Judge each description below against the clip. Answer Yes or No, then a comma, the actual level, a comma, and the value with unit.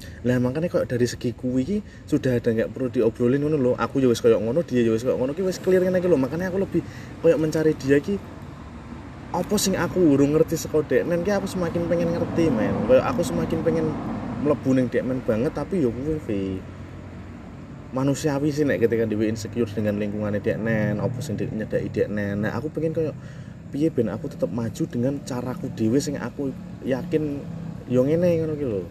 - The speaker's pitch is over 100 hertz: Yes, low, 135 Hz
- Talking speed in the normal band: No, fast, 160 wpm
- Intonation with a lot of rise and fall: Yes, wide, 5.8 semitones